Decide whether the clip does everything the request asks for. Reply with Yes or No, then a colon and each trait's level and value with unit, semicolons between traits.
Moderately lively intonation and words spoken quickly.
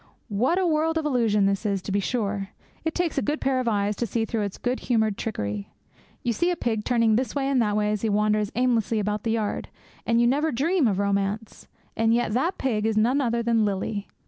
Yes: average, 3.6 semitones; fast, 235 wpm